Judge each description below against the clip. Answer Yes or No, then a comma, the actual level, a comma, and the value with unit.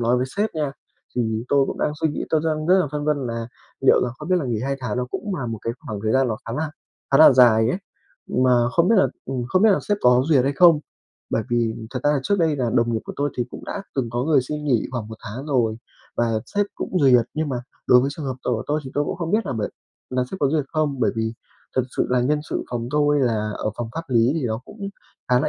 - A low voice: Yes, low, 130 Hz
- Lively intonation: No, average, 4.2 semitones